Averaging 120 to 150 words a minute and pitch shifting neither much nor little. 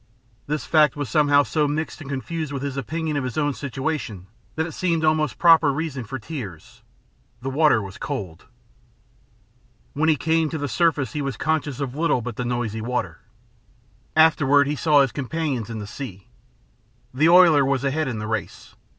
No: average, 185 wpm; average, 3.9 semitones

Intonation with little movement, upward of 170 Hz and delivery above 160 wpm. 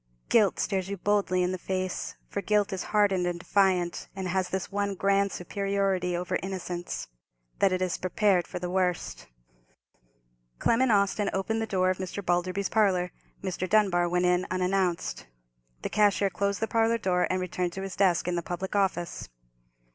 Yes: narrow, 1.9 semitones; medium, 185 Hz; average, 170 wpm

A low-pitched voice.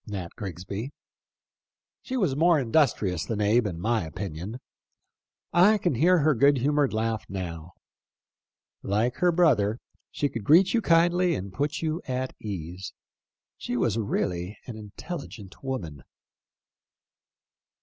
Yes: low, 115 Hz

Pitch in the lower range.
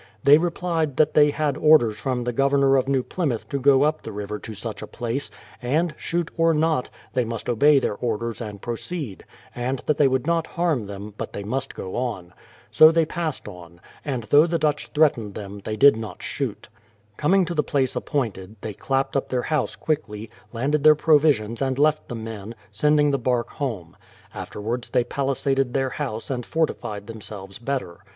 Yes: low, 130 Hz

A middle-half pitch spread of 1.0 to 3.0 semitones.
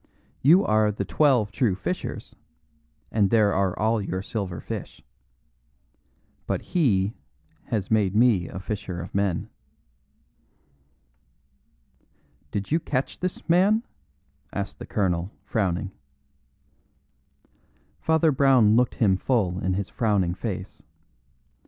No: average, 4.8 semitones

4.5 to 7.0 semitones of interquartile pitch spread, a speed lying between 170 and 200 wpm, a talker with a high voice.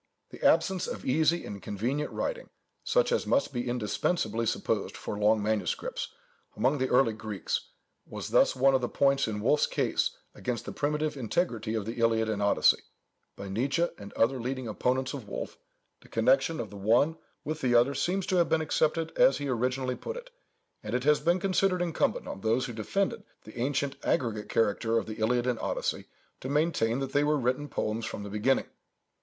No: average, 5.1 semitones; average, 190 wpm; low, 125 Hz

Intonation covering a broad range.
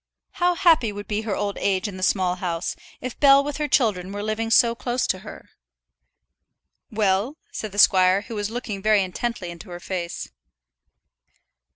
No: average, 4.2 semitones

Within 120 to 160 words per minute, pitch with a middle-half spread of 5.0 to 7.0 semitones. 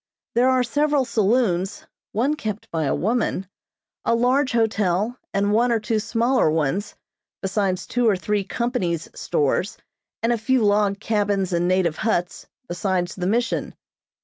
No: average, 150 wpm; average, 4.2 semitones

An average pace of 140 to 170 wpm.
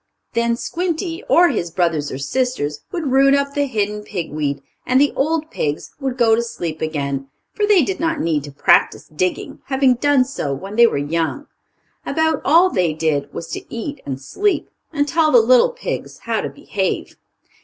No: average, 185 wpm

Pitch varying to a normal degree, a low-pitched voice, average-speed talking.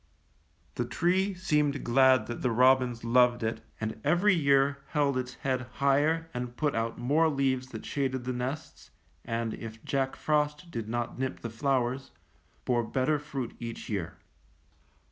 Yes: average, 3.3 semitones; low, 130 Hz; average, 155 wpm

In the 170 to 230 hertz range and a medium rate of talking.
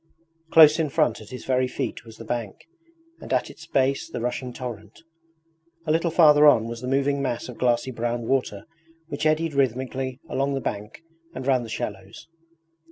No: low, 130 Hz; average, 180 wpm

